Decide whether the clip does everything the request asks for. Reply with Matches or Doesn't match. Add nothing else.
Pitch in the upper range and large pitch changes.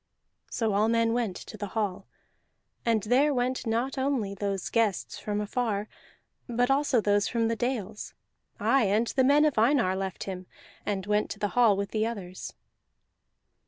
Doesn't match